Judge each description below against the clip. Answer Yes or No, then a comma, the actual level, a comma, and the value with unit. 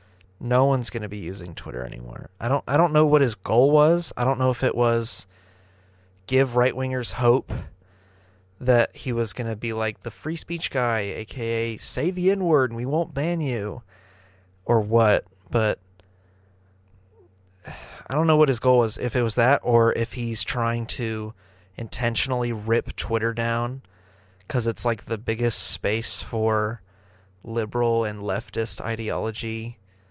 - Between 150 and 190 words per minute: Yes, average, 155 wpm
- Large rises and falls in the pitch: No, average, 4.5 semitones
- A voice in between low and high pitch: No, low, 115 Hz